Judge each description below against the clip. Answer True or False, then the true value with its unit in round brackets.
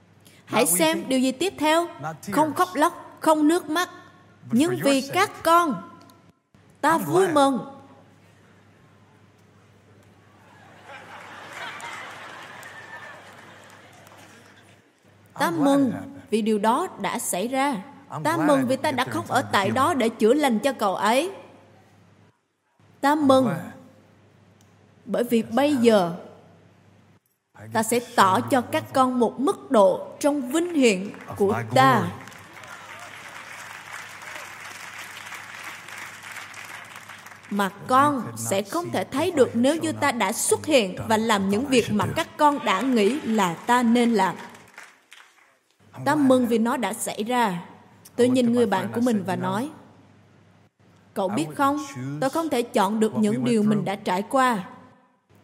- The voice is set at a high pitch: True (240 Hz)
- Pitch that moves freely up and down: True (6.3 semitones)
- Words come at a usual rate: False (125 wpm)